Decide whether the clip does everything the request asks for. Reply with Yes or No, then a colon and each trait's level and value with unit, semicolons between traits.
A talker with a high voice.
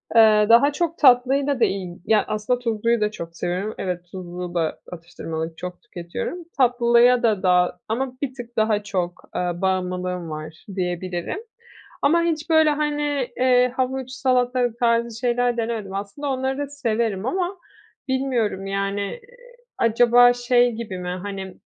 Yes: high, 230 Hz